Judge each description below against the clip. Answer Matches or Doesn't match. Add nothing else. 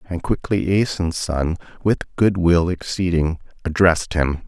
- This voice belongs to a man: Matches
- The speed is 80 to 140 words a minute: Matches